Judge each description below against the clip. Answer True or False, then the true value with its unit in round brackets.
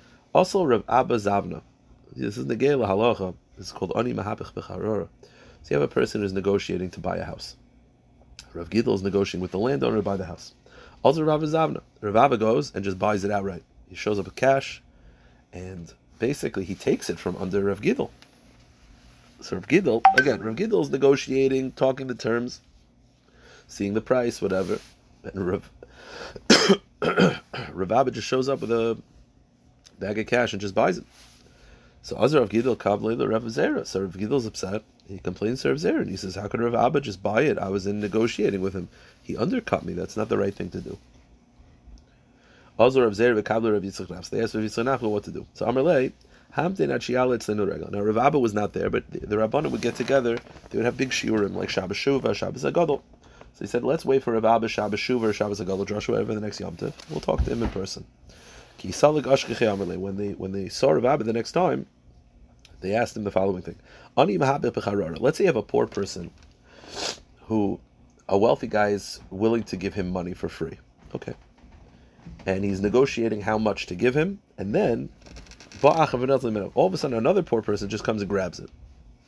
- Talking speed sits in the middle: True (190 wpm)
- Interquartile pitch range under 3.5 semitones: False (3.9 semitones)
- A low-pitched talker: True (105 Hz)